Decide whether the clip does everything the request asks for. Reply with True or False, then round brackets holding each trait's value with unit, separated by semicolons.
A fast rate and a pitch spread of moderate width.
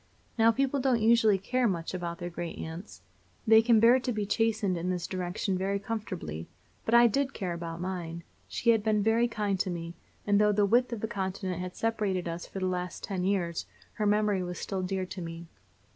True (210 wpm; 3.8 semitones)